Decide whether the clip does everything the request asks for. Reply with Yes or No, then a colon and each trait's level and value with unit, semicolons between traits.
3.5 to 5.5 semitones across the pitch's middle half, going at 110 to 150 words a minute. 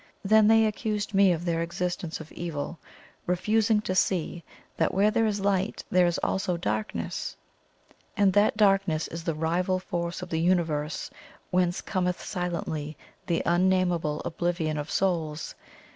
No: average, 3.0 semitones; average, 145 wpm